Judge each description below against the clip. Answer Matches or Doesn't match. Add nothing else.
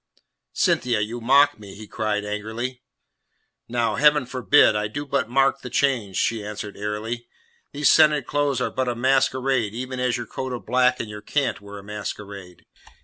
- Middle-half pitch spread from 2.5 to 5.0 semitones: Matches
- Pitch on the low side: Matches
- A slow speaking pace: Doesn't match